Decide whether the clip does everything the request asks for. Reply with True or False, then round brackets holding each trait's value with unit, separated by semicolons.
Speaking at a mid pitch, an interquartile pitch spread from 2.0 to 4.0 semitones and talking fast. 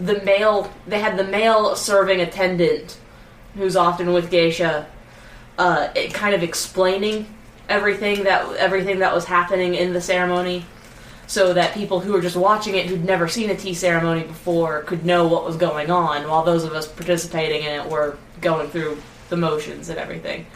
False (180 Hz; 2.8 semitones; 180 wpm)